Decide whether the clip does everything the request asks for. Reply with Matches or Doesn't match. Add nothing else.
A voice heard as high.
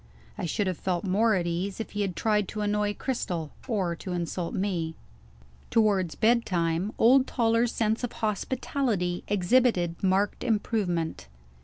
Matches